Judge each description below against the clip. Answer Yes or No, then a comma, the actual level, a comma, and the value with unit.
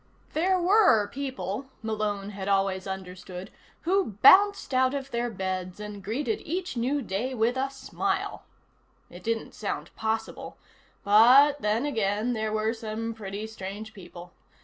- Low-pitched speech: No, high, 220 Hz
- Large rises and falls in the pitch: No, average, 5.0 semitones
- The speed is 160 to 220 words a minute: No, average, 140 wpm